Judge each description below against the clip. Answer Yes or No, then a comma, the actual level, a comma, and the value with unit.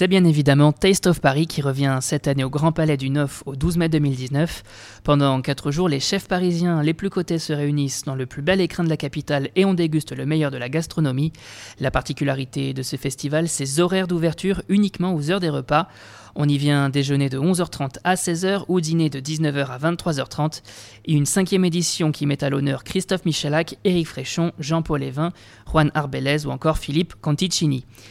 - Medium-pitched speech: Yes, medium, 150 Hz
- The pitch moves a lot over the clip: No, average, 3.6 semitones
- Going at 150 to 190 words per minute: No, average, 200 wpm